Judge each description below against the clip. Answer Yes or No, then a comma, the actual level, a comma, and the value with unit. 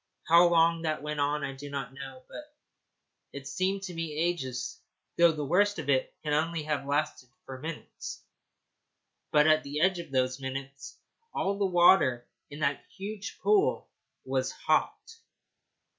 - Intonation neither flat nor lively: Yes, average, 4.0 semitones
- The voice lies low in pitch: No, medium, 150 Hz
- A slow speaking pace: No, average, 160 wpm